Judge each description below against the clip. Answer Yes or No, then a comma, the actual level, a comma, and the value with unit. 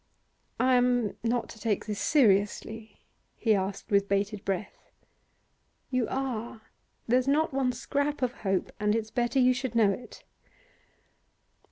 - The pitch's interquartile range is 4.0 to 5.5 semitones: No, average, 3.4 semitones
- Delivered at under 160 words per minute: Yes, average, 140 wpm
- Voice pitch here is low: No, high, 230 Hz